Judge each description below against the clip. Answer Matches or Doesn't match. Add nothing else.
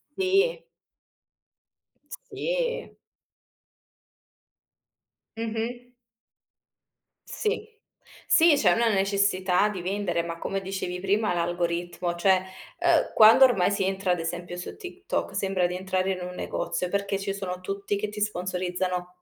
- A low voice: Doesn't match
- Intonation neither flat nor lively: Matches